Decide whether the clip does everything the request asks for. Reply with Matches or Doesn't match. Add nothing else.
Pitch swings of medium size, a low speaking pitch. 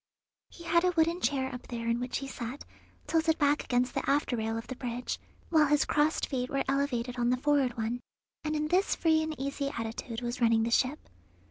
Doesn't match